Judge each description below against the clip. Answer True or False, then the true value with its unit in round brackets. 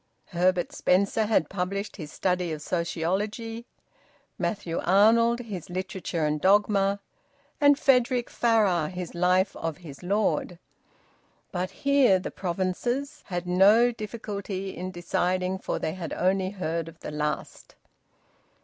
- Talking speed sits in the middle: False (125 wpm)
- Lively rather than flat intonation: False (3.3 semitones)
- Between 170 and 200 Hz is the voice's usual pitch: True (190 Hz)